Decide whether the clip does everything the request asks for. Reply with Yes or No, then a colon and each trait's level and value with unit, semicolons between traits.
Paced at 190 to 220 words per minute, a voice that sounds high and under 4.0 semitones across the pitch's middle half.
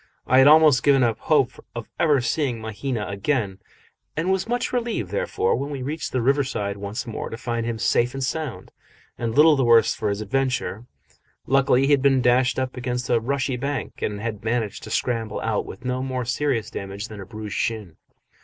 No: average, 200 wpm; low, 125 Hz; average, 3.6 semitones